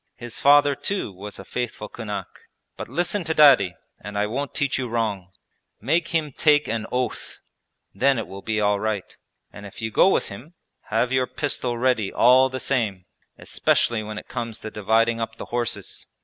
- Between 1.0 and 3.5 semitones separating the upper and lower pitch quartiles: No, average, 4.3 semitones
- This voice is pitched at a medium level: No, low, 115 Hz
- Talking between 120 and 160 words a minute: No, average, 185 wpm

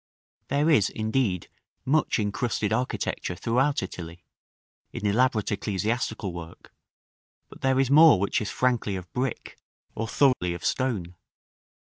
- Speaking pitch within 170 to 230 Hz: No, low, 110 Hz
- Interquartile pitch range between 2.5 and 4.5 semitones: No, wide, 5.4 semitones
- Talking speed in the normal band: No, slow, 125 wpm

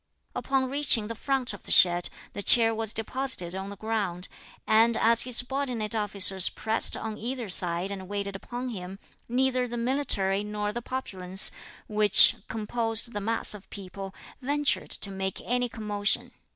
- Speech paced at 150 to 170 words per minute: Yes, average, 160 wpm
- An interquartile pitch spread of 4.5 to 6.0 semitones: No, average, 3.7 semitones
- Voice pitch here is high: Yes, high, 220 Hz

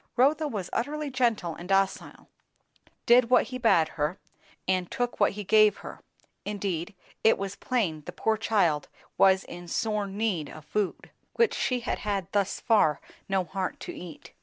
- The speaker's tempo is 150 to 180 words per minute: Yes, average, 165 wpm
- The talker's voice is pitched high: Yes, high, 200 Hz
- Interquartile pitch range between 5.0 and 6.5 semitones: No, average, 4.4 semitones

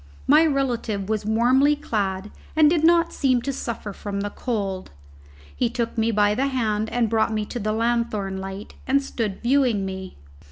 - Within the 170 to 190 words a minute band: Yes, average, 175 wpm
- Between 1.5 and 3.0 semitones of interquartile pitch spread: No, average, 4.2 semitones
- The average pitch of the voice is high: Yes, high, 230 Hz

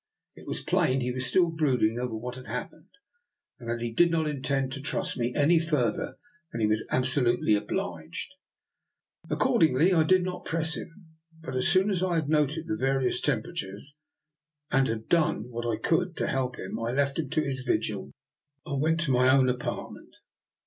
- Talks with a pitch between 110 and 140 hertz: Yes, low, 135 Hz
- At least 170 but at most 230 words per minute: Yes, average, 190 wpm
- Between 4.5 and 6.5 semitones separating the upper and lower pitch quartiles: Yes, average, 4.8 semitones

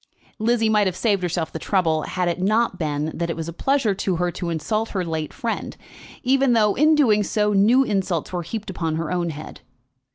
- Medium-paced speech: No, fast, 215 wpm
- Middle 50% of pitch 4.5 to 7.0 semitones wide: Yes, average, 4.8 semitones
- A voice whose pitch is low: No, high, 190 Hz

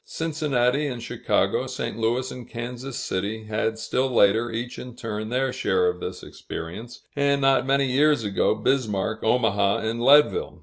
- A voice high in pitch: No, low, 120 Hz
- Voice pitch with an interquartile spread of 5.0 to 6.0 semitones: No, average, 3.5 semitones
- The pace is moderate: Yes, average, 160 wpm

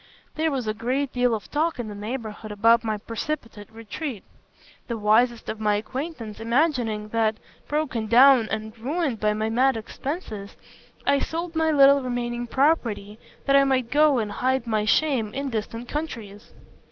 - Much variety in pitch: No, average, 4.3 semitones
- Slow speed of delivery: No, average, 165 wpm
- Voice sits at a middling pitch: No, high, 235 Hz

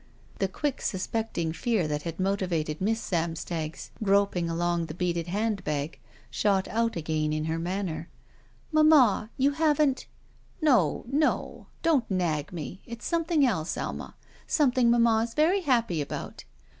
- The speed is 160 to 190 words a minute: No, average, 150 wpm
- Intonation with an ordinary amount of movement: No, wide, 6.5 semitones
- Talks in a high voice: Yes, high, 195 Hz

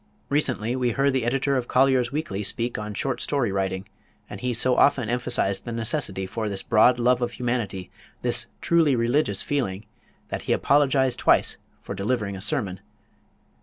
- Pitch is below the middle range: Yes, low, 120 Hz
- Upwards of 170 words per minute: No, average, 165 wpm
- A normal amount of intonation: Yes, average, 4.0 semitones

